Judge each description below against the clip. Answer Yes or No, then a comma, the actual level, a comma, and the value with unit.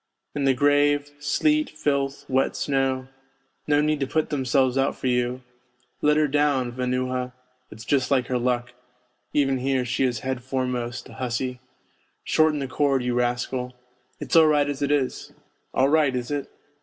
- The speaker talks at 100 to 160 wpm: No, average, 180 wpm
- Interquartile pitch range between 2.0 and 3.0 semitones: Yes, narrow, 2.4 semitones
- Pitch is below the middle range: Yes, low, 130 Hz